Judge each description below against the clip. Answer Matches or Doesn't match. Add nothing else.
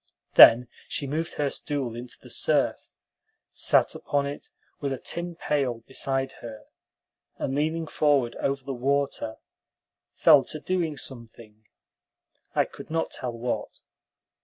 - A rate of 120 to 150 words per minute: Matches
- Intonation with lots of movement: Doesn't match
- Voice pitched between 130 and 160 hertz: Matches